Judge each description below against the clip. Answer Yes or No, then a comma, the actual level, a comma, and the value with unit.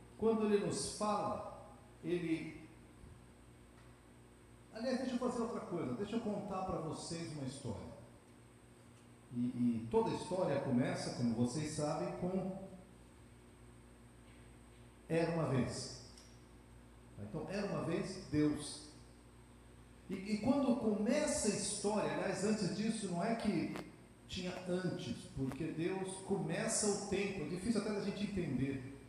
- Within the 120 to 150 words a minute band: Yes, average, 125 wpm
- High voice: No, medium, 160 Hz